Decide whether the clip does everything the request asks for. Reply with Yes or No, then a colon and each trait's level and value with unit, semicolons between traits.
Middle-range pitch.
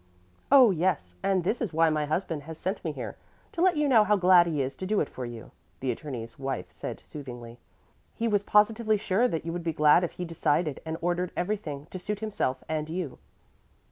Yes: medium, 170 Hz